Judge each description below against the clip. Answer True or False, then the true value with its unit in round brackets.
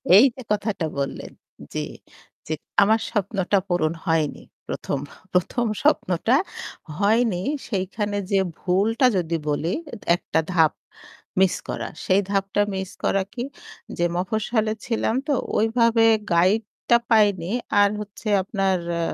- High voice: True (200 Hz)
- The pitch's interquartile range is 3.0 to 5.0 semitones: True (3.5 semitones)